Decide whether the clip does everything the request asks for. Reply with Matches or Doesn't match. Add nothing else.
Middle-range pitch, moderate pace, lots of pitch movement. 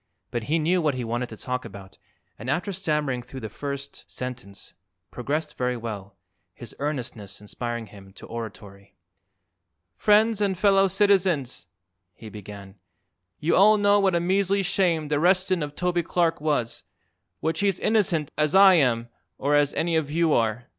Matches